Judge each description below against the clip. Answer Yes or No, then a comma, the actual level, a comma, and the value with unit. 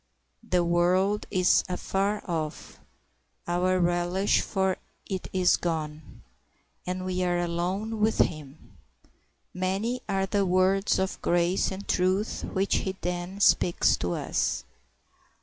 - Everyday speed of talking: No, slow, 120 wpm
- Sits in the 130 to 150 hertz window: No, medium, 185 Hz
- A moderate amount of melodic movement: No, narrow, 1.8 semitones